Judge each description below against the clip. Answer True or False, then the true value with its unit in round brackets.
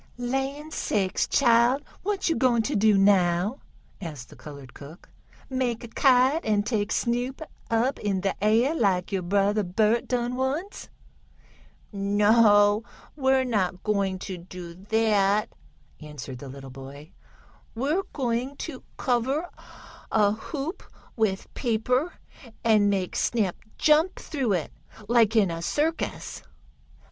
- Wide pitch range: False (5.0 semitones)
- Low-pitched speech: False (220 Hz)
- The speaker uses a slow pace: True (130 wpm)